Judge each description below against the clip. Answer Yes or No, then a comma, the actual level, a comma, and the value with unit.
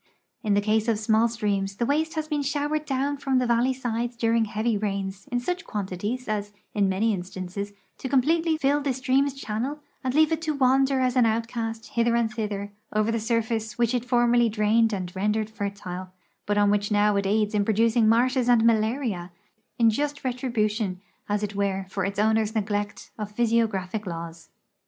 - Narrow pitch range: No, average, 3.5 semitones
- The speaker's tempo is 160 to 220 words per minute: Yes, average, 190 wpm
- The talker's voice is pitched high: Yes, high, 225 Hz